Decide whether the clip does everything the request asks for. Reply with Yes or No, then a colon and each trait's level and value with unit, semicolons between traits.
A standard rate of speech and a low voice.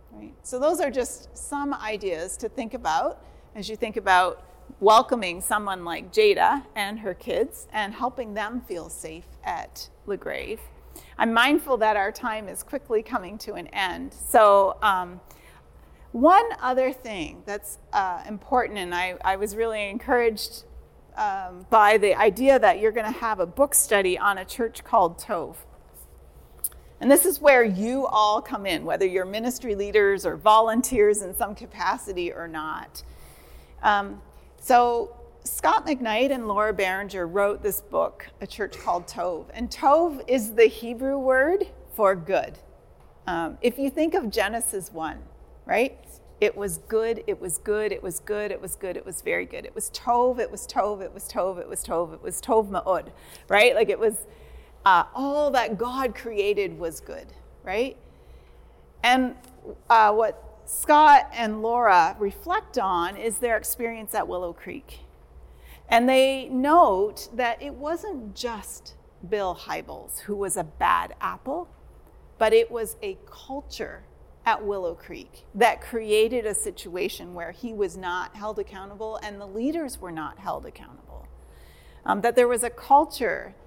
No: average, 160 wpm; high, 220 Hz